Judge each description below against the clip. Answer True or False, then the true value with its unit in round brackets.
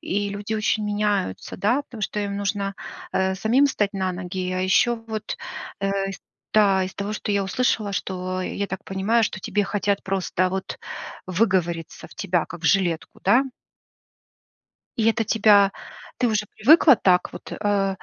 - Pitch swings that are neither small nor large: False (2.1 semitones)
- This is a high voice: True (200 Hz)